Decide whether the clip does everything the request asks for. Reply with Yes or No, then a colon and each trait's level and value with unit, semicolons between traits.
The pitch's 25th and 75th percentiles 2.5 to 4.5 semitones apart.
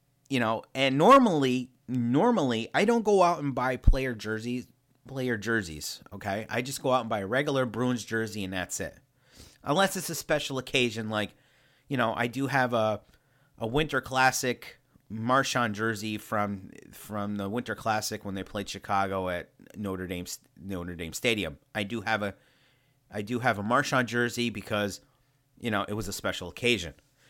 Yes: average, 4.1 semitones